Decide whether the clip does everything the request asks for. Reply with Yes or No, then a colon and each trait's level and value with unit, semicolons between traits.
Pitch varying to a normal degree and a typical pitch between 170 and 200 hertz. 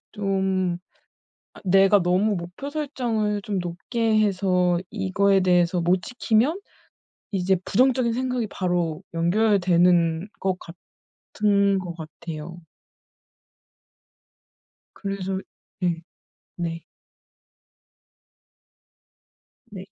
Yes: average, 3.2 semitones; high, 190 Hz